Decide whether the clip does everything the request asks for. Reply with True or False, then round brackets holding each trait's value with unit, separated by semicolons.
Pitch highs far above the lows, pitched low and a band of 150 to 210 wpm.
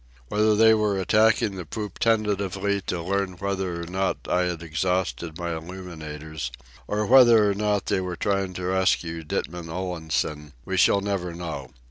False (3.2 semitones; 95 Hz; 160 wpm)